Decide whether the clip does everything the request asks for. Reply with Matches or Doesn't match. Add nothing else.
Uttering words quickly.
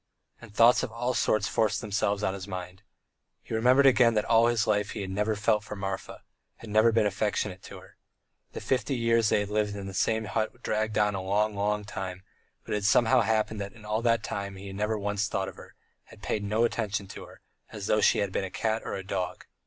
Matches